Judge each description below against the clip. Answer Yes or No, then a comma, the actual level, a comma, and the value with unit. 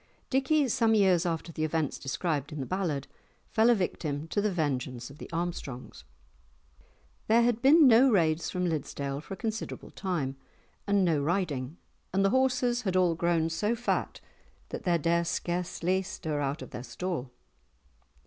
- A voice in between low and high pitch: Yes, medium, 175 Hz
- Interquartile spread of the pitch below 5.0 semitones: No, wide, 5.5 semitones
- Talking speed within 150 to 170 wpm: Yes, average, 165 wpm